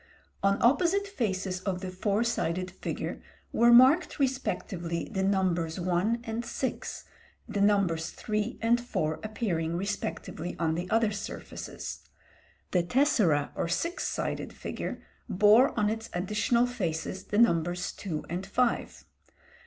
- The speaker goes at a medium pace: No, slow, 130 wpm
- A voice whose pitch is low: No, high, 200 Hz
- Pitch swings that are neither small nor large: Yes, average, 5.0 semitones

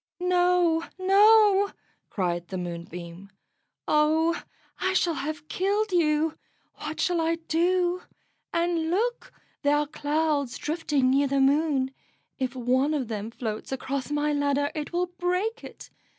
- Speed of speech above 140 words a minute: No, slow, 135 wpm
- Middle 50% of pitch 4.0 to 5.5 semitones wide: Yes, average, 4.8 semitones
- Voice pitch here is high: Yes, very high, 305 Hz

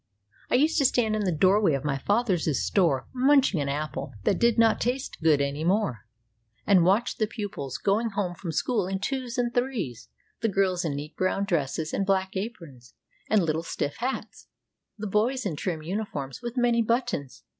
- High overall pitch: Yes, high, 195 Hz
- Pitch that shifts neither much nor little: No, wide, 7.0 semitones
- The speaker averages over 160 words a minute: Yes, average, 185 wpm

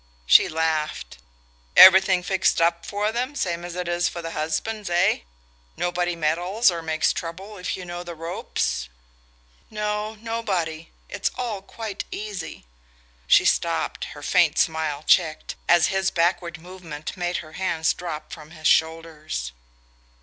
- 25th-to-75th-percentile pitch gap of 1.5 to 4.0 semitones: Yes, average, 3.0 semitones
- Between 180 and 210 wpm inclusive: No, average, 140 wpm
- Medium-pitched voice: Yes, medium, 175 Hz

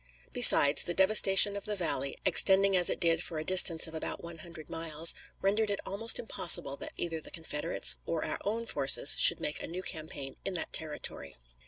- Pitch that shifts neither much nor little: Yes, average, 3.7 semitones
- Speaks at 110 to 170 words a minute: No, average, 195 wpm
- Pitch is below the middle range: No, medium, 170 Hz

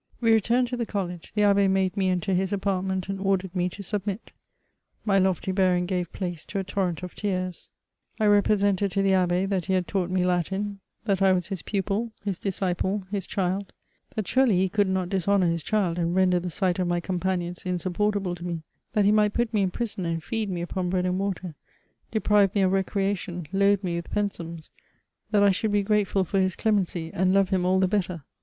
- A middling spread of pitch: No, narrow, 2.0 semitones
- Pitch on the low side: No, high, 190 Hz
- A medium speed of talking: No, fast, 215 wpm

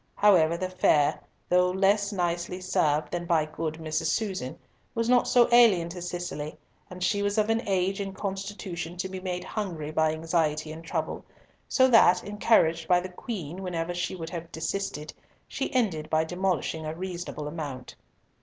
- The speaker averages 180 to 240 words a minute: No, average, 165 wpm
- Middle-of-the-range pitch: Yes, medium, 175 Hz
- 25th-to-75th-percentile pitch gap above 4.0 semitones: No, average, 3.3 semitones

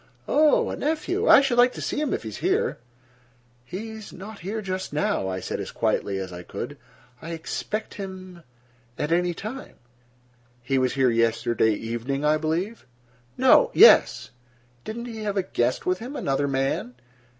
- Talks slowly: No, average, 165 wpm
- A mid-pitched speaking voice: Yes, medium, 170 Hz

